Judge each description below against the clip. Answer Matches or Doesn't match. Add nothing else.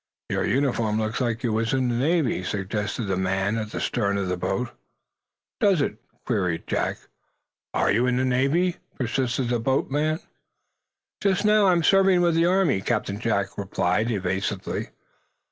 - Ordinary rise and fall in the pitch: Doesn't match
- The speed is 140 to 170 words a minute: Matches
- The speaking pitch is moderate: Doesn't match